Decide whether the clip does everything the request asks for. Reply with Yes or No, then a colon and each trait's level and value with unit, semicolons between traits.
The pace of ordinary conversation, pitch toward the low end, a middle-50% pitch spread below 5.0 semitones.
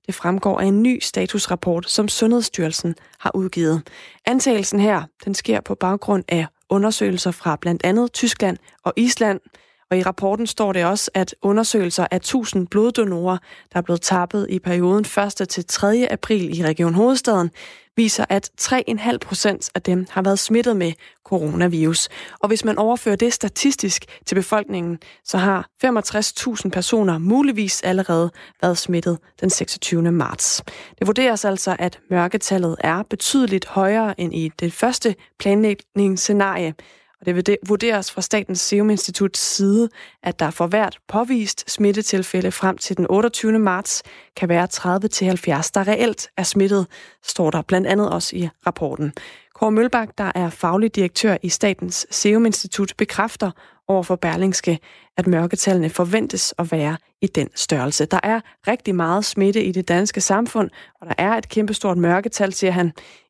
No: average, 155 wpm; high, 195 Hz; average, 3.1 semitones